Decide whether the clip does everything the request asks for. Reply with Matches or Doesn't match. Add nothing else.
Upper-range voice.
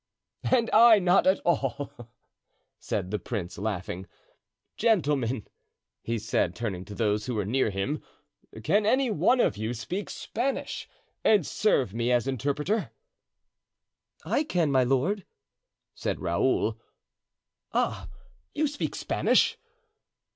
Doesn't match